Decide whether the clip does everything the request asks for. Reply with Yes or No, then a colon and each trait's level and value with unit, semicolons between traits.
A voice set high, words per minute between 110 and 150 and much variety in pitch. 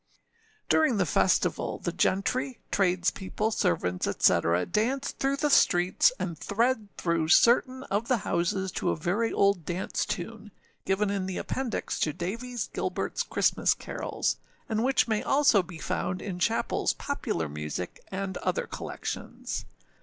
Yes: high, 200 Hz; average, 145 wpm; wide, 5.8 semitones